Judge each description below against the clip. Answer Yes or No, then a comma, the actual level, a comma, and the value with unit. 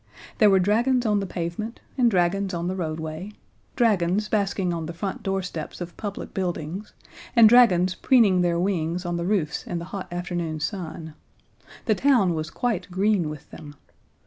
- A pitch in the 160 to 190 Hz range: Yes, medium, 185 Hz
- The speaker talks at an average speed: Yes, average, 170 wpm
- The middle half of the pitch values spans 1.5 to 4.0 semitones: Yes, average, 3.5 semitones